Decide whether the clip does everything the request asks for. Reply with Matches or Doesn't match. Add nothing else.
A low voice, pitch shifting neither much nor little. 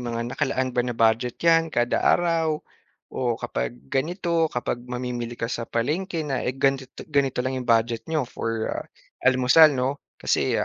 Matches